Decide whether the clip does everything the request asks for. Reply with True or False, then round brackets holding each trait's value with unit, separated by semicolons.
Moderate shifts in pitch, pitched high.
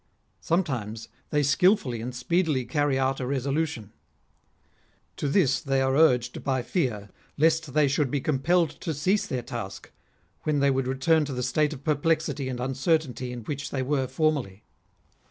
False (3.5 semitones; 135 Hz)